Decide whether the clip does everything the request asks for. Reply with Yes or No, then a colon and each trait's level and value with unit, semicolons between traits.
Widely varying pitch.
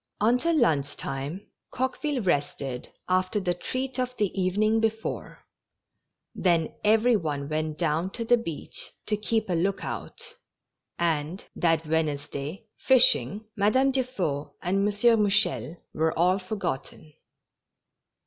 Yes: wide, 6.0 semitones